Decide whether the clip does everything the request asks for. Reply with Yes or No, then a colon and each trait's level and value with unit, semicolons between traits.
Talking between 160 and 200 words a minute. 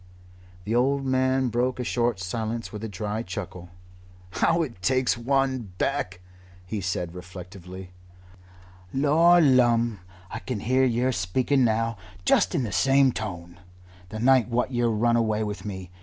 No: average, 150 wpm